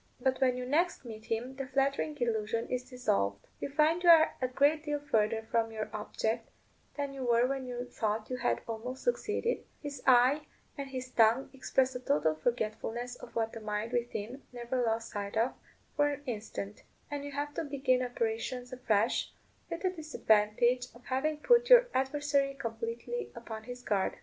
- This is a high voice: Yes, very high, 250 Hz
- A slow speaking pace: No, average, 180 wpm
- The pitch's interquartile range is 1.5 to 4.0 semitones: Yes, average, 3.7 semitones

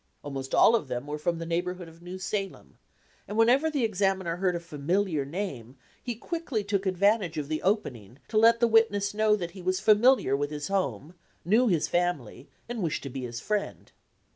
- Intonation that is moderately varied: No, wide, 5.8 semitones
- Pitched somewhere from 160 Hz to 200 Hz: Yes, medium, 185 Hz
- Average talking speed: Yes, average, 195 wpm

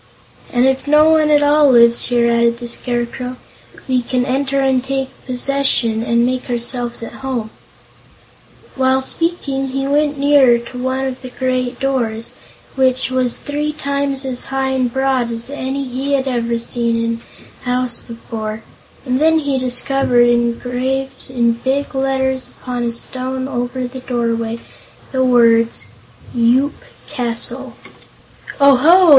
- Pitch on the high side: Yes, very high, 255 Hz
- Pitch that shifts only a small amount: Yes, narrow, 2.1 semitones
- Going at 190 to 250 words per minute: No, average, 145 wpm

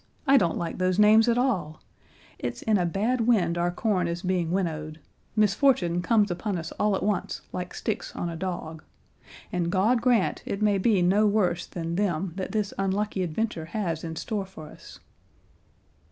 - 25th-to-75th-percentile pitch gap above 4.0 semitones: No, average, 3.7 semitones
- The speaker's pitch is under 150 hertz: No, high, 190 Hz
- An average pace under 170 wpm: No, average, 180 wpm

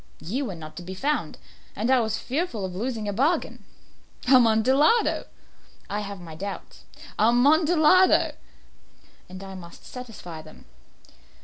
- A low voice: No, high, 220 Hz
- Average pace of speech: No, slow, 130 wpm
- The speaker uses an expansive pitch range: Yes, wide, 6.2 semitones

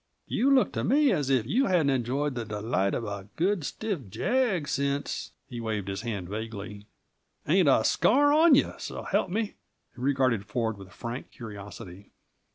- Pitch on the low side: Yes, low, 125 Hz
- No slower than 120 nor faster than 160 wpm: No, average, 175 wpm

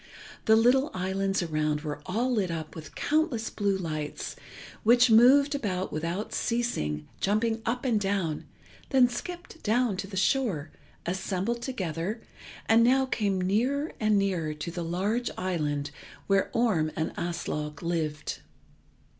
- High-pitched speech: Yes, high, 195 Hz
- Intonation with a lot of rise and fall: Yes, wide, 6.1 semitones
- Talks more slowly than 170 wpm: Yes, average, 140 wpm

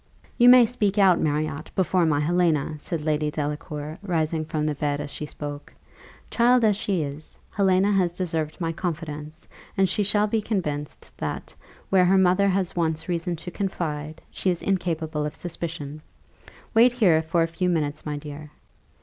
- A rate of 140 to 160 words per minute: No, average, 170 wpm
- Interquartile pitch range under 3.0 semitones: No, average, 3.9 semitones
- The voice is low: No, medium, 165 Hz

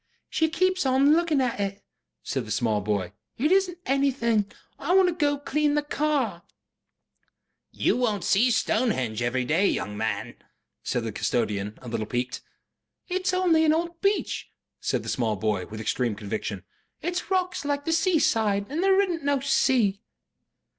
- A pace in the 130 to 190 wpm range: Yes, average, 165 wpm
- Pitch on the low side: No, very high, 250 Hz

